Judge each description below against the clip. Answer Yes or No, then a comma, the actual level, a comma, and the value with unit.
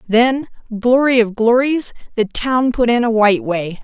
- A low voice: No, high, 235 Hz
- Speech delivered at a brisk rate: No, average, 170 wpm